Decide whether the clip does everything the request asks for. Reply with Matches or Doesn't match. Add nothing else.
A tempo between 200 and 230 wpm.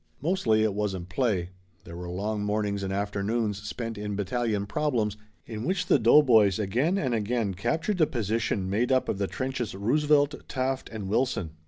Doesn't match